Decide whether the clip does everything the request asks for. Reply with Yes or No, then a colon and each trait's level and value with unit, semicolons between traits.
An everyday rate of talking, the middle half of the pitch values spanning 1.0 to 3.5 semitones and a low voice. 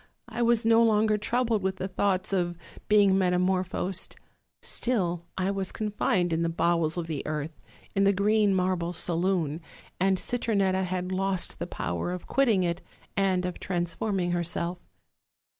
No: average, 155 wpm; narrow, 2.5 semitones; medium, 185 Hz